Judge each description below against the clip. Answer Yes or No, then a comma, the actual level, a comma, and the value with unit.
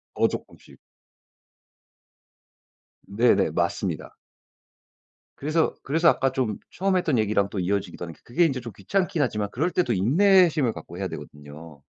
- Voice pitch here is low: Yes, low, 120 Hz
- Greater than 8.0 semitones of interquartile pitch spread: Yes, wide, 8.6 semitones